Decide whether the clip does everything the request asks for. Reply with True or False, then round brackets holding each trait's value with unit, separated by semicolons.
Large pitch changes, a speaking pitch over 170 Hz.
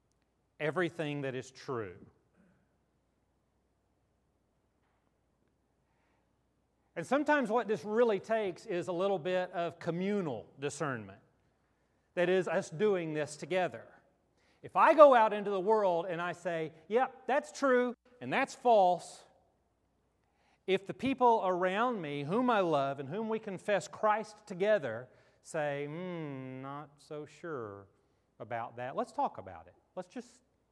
True (7.2 semitones; 180 Hz)